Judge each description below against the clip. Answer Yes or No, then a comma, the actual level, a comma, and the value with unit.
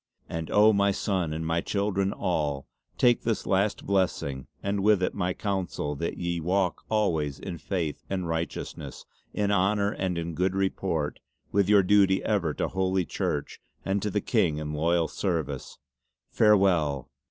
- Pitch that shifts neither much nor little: Yes, average, 3.5 semitones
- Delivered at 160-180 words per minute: Yes, average, 165 wpm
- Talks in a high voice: No, very low, 95 Hz